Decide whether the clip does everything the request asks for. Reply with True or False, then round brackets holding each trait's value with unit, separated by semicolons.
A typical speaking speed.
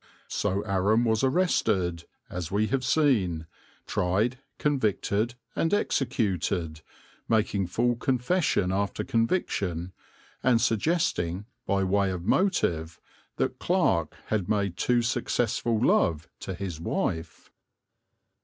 False (105 wpm)